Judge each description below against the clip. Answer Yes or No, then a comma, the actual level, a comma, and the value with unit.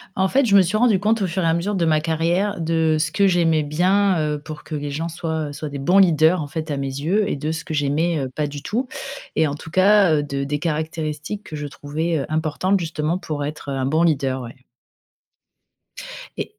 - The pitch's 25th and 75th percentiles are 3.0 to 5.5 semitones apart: Yes, average, 3.5 semitones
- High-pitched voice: No, medium, 160 Hz